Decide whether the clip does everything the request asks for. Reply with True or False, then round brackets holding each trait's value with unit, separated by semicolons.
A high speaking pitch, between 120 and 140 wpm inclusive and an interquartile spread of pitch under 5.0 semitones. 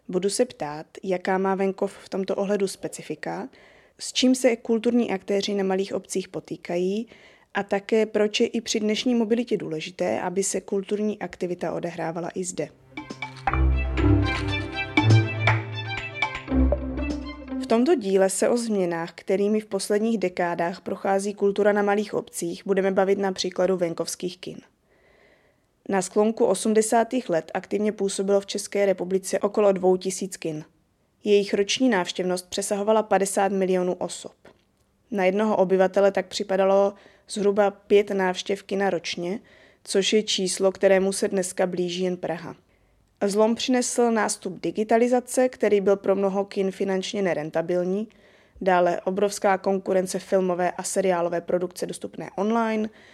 True (195 Hz; 130 wpm; 2.4 semitones)